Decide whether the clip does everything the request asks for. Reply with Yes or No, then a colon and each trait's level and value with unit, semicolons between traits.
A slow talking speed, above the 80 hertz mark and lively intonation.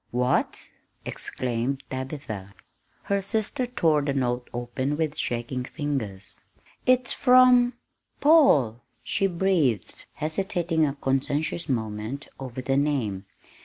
Yes: slow, 105 wpm; medium, 140 Hz; wide, 6.1 semitones